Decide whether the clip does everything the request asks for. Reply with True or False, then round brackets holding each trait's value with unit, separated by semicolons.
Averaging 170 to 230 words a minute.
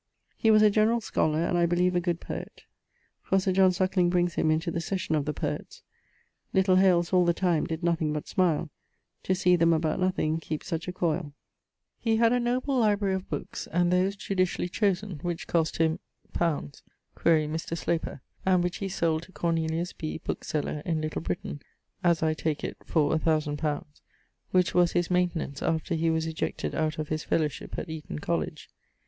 True (190 wpm)